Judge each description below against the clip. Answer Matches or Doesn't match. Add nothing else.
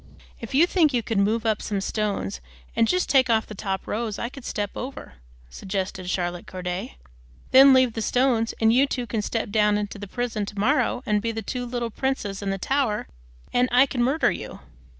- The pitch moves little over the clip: Doesn't match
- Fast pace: Matches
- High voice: Matches